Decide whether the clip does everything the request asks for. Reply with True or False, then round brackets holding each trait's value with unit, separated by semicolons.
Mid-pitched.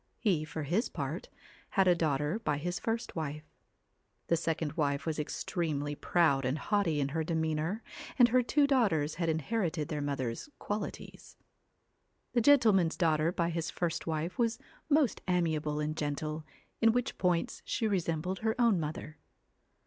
True (165 Hz)